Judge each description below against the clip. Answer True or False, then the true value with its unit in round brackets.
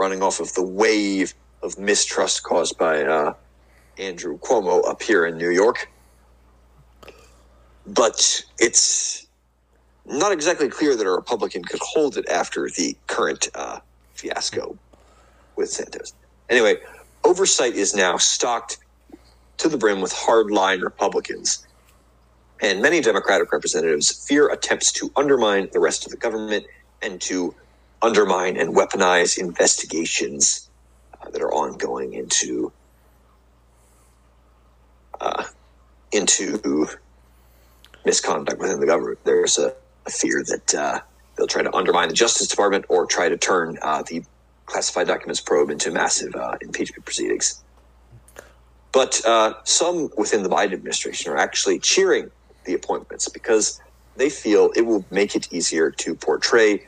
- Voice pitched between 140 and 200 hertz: False (110 Hz)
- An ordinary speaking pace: False (130 wpm)